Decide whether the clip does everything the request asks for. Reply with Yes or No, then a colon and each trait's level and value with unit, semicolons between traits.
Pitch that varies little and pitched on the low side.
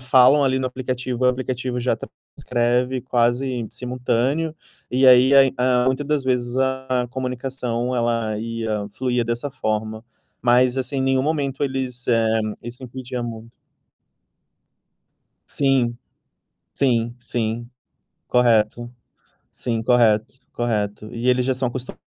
Yes: narrow, 1.7 semitones; low, 125 Hz